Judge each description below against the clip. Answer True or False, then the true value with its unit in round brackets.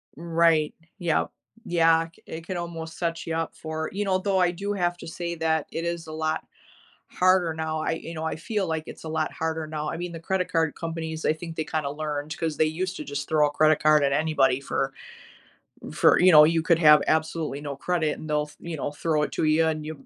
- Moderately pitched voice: True (160 Hz)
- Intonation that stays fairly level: True (1.5 semitones)